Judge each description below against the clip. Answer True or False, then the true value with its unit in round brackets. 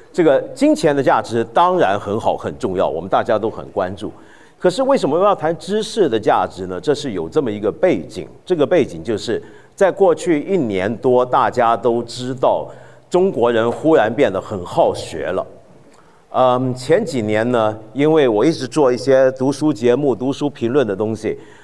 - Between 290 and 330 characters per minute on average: False (265 characters per minute)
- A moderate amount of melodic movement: False (5.7 semitones)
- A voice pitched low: True (130 Hz)